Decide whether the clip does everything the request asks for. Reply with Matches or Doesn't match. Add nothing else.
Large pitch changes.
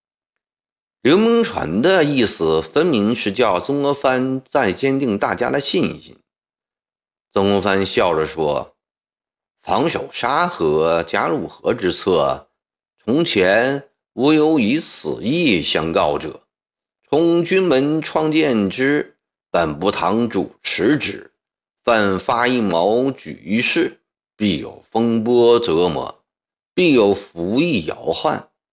Matches